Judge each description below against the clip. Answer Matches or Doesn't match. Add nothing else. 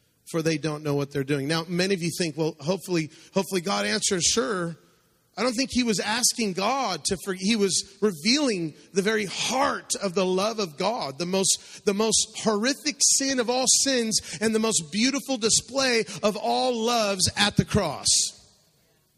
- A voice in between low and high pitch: Doesn't match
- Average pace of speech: Matches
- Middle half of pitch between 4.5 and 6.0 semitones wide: Matches